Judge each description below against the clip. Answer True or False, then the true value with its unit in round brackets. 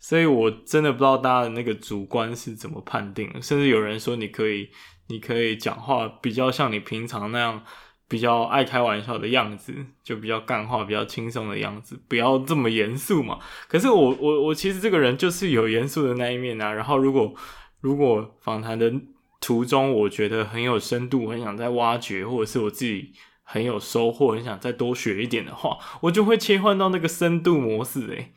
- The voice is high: False (120 Hz)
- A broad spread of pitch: False (3.6 semitones)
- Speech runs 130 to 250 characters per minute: False (305 characters per minute)